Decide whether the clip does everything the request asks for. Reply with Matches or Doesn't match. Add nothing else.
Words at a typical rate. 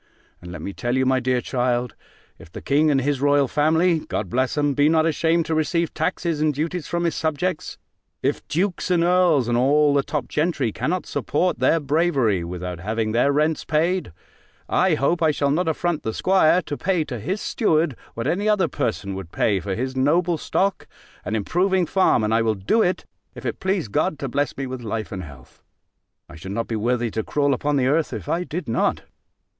Doesn't match